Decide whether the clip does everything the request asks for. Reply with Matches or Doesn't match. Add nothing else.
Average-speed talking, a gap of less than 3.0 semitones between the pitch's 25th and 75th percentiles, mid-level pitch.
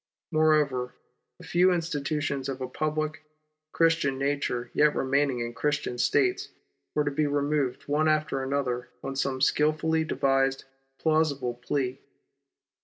Doesn't match